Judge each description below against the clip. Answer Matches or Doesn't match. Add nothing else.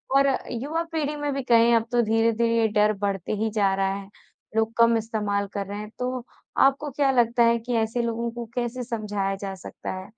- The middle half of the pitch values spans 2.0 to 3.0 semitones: Matches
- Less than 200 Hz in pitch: Doesn't match